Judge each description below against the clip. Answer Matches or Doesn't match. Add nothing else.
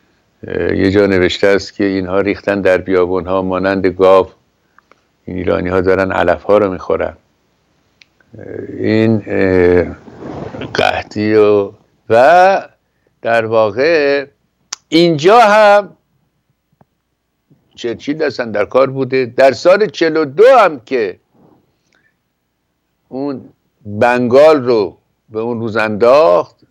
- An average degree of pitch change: Doesn't match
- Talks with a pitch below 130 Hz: Matches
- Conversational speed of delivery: Doesn't match